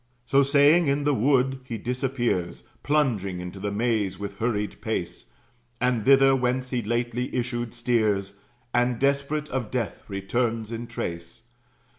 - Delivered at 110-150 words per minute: Yes, average, 140 wpm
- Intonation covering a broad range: No, average, 4.2 semitones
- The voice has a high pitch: No, low, 120 Hz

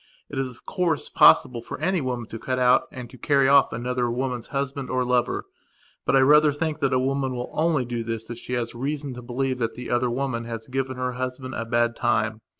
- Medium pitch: No, low, 125 Hz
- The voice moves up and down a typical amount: No, narrow, 2.2 semitones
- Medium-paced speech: No, fast, 235 wpm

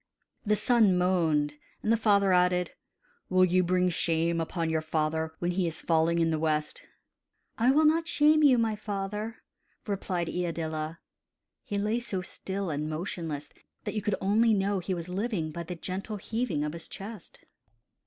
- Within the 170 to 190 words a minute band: Yes, average, 175 wpm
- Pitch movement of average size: Yes, average, 4.4 semitones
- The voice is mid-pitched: Yes, medium, 180 Hz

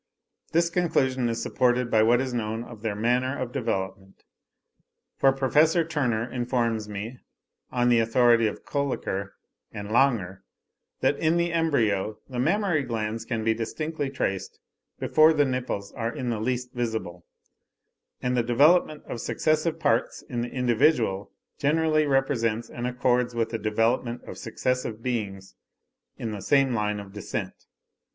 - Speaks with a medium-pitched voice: No, low, 120 Hz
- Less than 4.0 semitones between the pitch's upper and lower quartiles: Yes, average, 3.4 semitones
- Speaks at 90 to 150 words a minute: Yes, average, 145 wpm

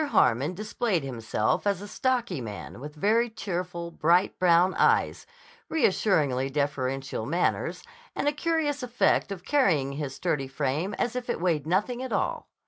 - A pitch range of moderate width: No, wide, 8.0 semitones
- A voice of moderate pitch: Yes, medium, 175 Hz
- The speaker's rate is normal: Yes, average, 150 wpm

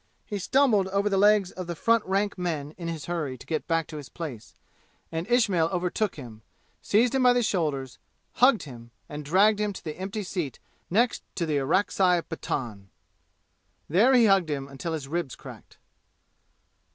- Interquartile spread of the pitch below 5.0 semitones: No, wide, 5.4 semitones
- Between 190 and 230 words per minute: No, average, 175 wpm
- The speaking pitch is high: No, medium, 175 Hz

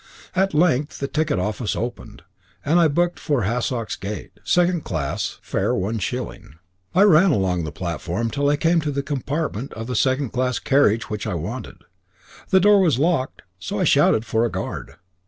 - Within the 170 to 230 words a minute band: Yes, average, 180 wpm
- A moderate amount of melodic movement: No, wide, 6.6 semitones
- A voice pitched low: Yes, low, 130 Hz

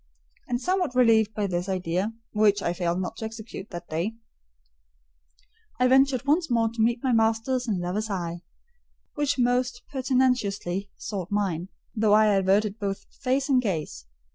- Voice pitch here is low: No, high, 220 Hz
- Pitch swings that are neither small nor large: Yes, average, 4.6 semitones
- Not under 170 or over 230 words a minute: No, average, 155 wpm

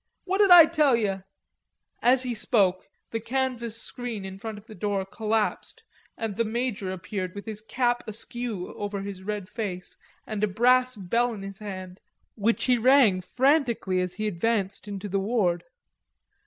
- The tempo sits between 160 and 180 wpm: Yes, average, 170 wpm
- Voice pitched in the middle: No, high, 215 Hz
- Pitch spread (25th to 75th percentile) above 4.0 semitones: No, average, 3.7 semitones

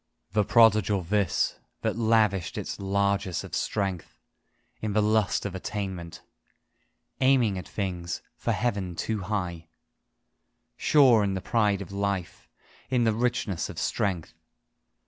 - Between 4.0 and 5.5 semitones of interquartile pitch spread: No, average, 2.7 semitones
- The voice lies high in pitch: No, low, 100 Hz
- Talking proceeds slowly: Yes, slow, 125 wpm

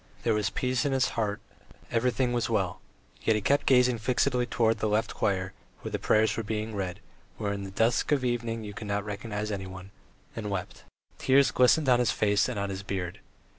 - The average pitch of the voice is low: Yes, low, 110 Hz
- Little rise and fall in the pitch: No, average, 3.3 semitones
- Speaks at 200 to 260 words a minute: Yes, fast, 205 wpm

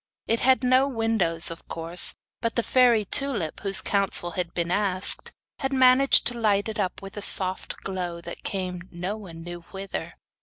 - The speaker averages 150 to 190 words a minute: Yes, average, 180 wpm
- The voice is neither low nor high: No, high, 195 Hz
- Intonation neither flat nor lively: Yes, average, 4.8 semitones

